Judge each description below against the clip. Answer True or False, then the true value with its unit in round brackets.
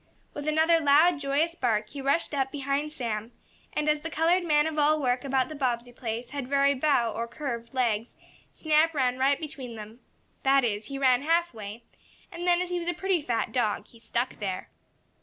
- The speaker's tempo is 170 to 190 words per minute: False (200 wpm)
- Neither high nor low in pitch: False (275 Hz)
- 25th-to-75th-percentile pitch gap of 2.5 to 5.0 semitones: True (4.3 semitones)